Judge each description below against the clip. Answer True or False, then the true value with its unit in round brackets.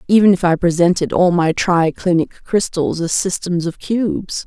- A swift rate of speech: False (175 wpm)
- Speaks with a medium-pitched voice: True (175 Hz)